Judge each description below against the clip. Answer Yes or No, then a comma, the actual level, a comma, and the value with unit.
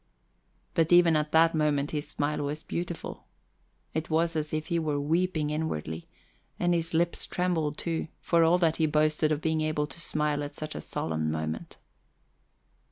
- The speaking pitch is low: No, medium, 155 Hz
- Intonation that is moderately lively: No, narrow, 1.9 semitones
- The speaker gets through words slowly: No, average, 170 wpm